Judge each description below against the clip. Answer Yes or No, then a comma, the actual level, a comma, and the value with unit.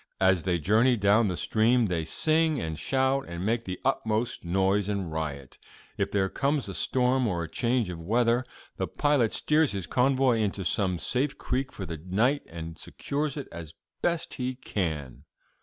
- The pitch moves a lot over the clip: Yes, wide, 6.6 semitones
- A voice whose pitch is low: Yes, low, 110 Hz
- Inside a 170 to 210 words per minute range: Yes, average, 175 wpm